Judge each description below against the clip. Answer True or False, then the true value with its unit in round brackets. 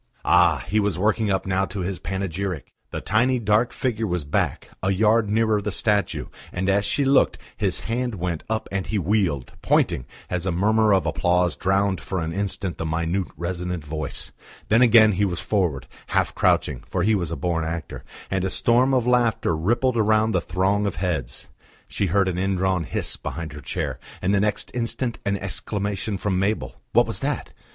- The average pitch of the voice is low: True (95 Hz)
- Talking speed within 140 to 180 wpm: False (190 wpm)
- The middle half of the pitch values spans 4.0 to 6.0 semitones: False (3.4 semitones)